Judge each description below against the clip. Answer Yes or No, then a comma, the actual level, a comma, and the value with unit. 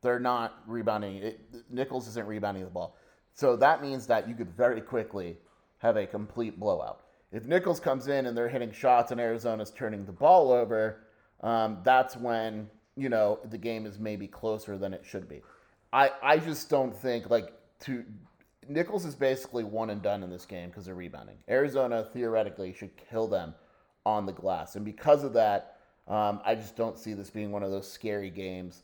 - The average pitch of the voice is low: Yes, low, 110 Hz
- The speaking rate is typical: Yes, average, 190 wpm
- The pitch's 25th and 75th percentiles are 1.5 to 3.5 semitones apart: Yes, average, 3.1 semitones